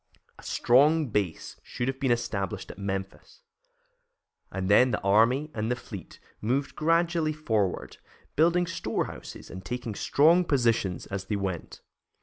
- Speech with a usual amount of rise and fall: No, wide, 7.3 semitones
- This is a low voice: Yes, low, 120 Hz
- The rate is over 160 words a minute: No, slow, 135 wpm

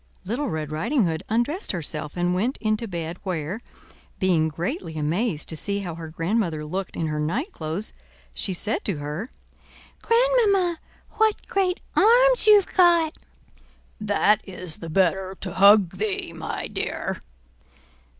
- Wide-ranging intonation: Yes, wide, 7.6 semitones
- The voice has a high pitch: Yes, high, 195 Hz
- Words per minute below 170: Yes, average, 140 wpm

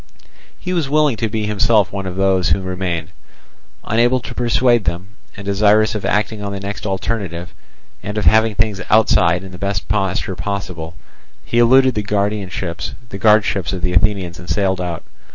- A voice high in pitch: No, low, 100 Hz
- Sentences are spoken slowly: No, average, 170 wpm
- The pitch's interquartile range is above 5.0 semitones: No, average, 2.8 semitones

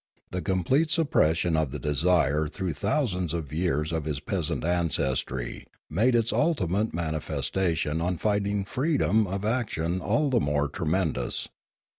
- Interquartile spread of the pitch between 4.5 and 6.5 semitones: Yes, average, 4.9 semitones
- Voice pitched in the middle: No, very low, 90 Hz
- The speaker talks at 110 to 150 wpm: Yes, average, 140 wpm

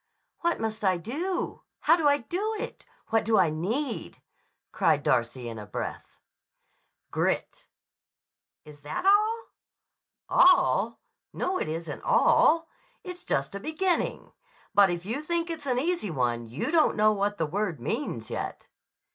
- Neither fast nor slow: Yes, average, 145 wpm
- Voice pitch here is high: Yes, high, 220 Hz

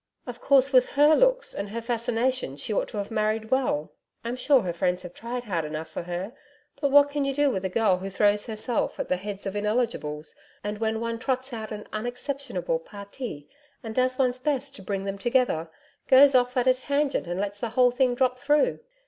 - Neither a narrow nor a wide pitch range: Yes, average, 4.5 semitones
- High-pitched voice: Yes, high, 230 Hz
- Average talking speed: No, fast, 215 wpm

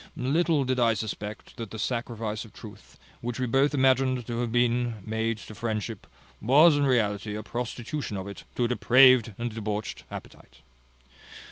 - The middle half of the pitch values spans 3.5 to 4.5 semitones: No, average, 2.7 semitones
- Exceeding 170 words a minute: No, average, 165 wpm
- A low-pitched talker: Yes, low, 120 Hz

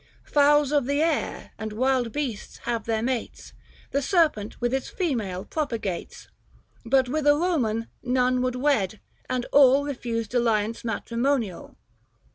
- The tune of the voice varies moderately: Yes, average, 3.8 semitones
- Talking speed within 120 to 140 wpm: Yes, slow, 135 wpm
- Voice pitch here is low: No, very high, 250 Hz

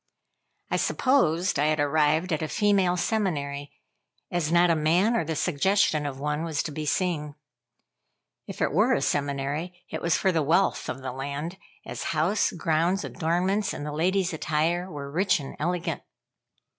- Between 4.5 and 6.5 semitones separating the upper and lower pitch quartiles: No, average, 3.5 semitones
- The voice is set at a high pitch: No, medium, 160 Hz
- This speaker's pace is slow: No, average, 170 wpm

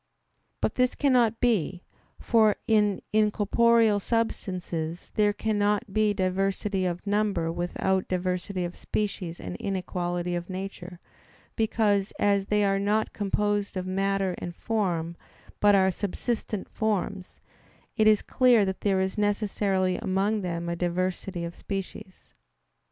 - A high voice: Yes, high, 195 Hz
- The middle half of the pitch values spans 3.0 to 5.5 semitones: No, narrow, 2.4 semitones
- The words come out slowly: Yes, slow, 130 wpm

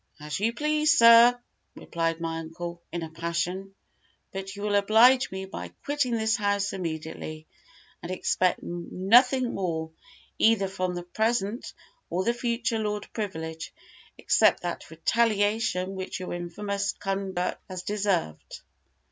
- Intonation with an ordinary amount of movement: Yes, average, 4.3 semitones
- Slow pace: Yes, slow, 130 wpm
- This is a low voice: No, high, 195 Hz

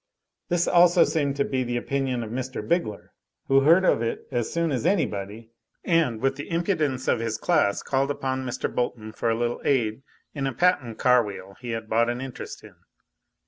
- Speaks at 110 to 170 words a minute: No, average, 195 wpm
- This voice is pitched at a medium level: No, low, 130 Hz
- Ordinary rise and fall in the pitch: Yes, average, 4.2 semitones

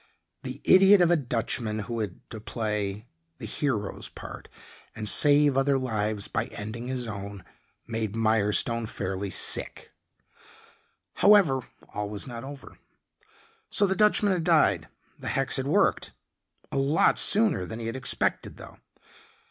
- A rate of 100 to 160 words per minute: Yes, average, 140 wpm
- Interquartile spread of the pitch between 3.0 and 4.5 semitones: No, average, 5.2 semitones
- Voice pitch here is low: Yes, low, 115 Hz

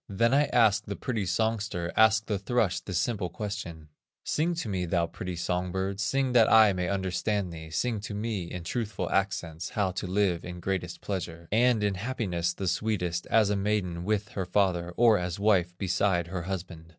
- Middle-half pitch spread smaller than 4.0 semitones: Yes, average, 3.4 semitones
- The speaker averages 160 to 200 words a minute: Yes, average, 190 wpm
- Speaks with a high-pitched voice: No, very low, 95 Hz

